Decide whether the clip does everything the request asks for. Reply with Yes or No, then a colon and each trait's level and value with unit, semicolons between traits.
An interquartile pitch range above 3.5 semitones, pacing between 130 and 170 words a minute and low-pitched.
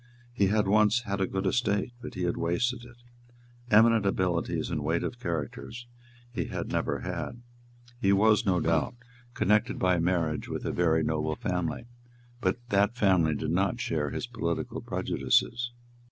Yes: average, 4.8 semitones; average, 160 wpm; very low, 95 Hz